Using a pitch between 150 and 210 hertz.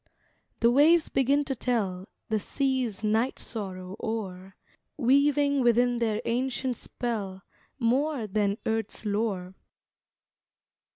No: high, 230 Hz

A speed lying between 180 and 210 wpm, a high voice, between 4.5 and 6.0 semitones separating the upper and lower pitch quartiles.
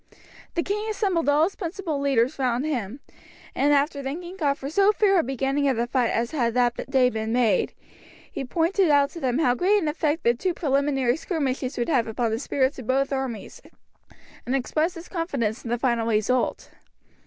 Yes: average, 195 wpm; very high, 275 Hz; average, 4.9 semitones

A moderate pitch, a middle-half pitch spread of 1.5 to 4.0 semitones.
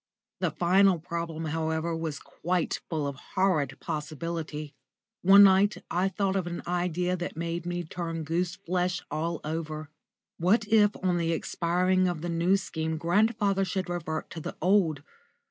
Yes: medium, 170 Hz; narrow, 2.5 semitones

